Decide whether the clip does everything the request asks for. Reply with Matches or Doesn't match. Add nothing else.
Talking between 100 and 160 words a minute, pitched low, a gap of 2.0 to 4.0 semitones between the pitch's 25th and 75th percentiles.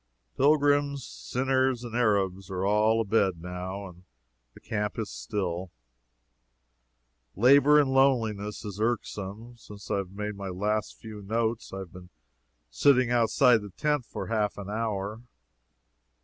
Matches